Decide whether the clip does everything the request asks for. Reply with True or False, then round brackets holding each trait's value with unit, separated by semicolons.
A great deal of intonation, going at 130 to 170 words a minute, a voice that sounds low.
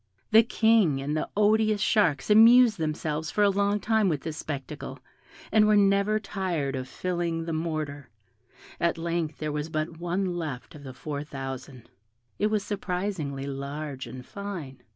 False (5.9 semitones; 160 wpm; 165 Hz)